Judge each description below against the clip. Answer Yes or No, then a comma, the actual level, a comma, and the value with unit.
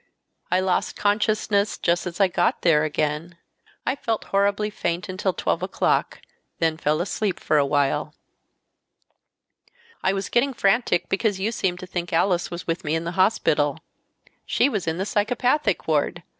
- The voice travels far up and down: No, average, 3.7 semitones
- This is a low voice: No, medium, 185 Hz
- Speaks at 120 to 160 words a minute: Yes, average, 155 wpm